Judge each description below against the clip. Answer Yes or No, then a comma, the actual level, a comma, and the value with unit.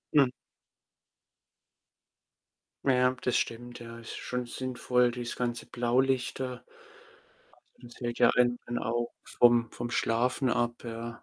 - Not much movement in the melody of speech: Yes, narrow, 1.0 semitones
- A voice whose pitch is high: No, low, 120 Hz